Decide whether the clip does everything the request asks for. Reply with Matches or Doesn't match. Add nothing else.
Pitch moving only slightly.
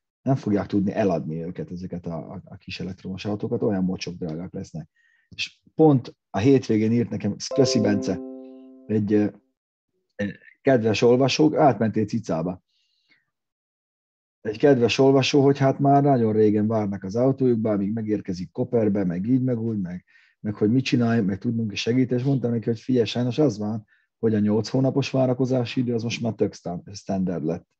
Doesn't match